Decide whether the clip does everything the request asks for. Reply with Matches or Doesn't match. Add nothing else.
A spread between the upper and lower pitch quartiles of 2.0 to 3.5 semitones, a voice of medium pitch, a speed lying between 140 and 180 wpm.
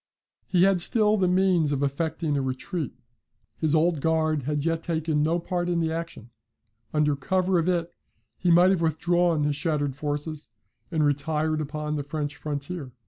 Matches